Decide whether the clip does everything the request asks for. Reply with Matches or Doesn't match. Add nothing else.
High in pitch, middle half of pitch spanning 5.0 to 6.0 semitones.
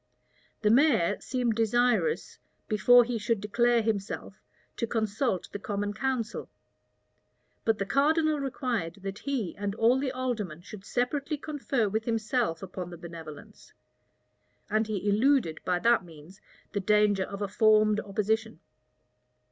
Doesn't match